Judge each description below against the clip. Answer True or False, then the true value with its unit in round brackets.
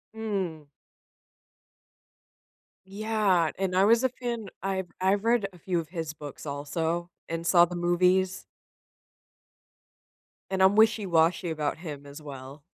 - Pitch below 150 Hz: False (180 Hz)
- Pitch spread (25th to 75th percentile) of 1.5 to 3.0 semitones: False (3.6 semitones)